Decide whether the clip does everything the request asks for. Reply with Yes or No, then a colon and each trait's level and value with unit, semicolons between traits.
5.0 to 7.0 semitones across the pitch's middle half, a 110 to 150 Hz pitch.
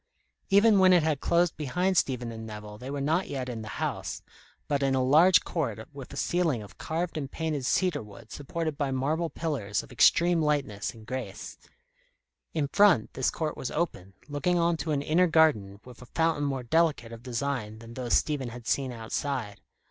Yes: average, 5.3 semitones; medium, 140 Hz